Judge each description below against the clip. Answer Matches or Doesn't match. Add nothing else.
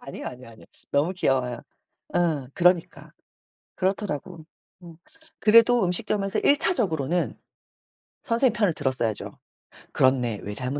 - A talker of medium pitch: Matches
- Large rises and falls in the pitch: Matches